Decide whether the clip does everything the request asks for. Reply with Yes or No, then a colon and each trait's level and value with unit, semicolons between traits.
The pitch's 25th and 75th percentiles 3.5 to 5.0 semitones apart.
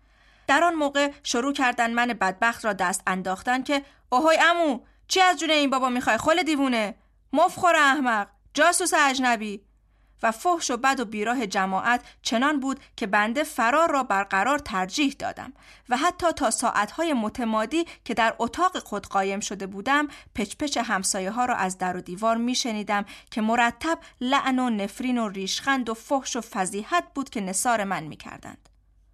No: wide, 5.5 semitones